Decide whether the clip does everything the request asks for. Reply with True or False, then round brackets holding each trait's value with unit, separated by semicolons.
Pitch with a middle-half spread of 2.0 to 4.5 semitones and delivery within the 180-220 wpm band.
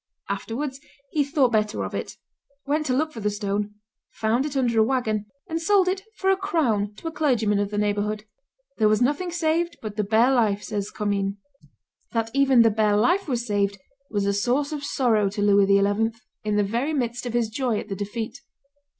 False (5.0 semitones; 200 wpm)